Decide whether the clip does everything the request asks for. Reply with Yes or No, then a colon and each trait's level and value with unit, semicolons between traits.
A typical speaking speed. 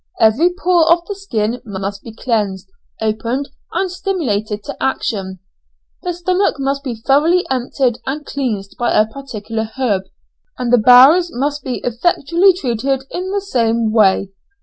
Yes: average, 150 wpm